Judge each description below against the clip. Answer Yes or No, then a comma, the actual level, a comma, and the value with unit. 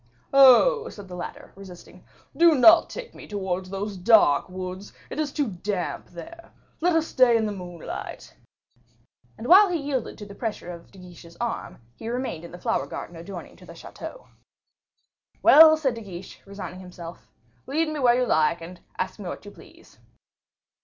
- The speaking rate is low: No, average, 175 wpm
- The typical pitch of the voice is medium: No, high, 205 Hz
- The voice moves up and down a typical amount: No, wide, 7.5 semitones